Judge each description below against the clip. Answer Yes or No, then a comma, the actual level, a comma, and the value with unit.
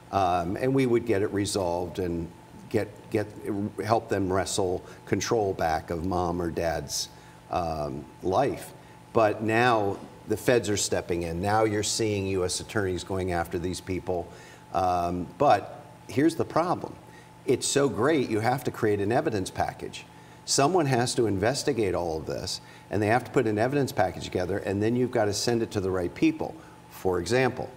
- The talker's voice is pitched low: Yes, low, 100 Hz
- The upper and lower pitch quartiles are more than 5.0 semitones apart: No, average, 3.9 semitones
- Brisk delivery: No, average, 175 wpm